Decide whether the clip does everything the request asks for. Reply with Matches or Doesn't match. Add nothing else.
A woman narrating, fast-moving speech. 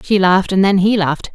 Matches